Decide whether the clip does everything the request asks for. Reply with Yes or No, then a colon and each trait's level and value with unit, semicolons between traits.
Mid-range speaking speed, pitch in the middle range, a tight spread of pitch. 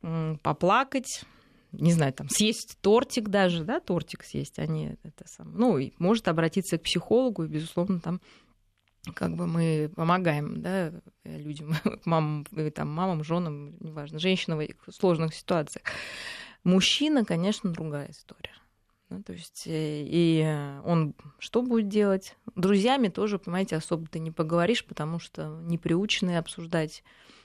No: average, 135 wpm; medium, 170 Hz; average, 3.8 semitones